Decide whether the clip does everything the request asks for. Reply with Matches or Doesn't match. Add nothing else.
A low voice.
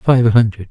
Matches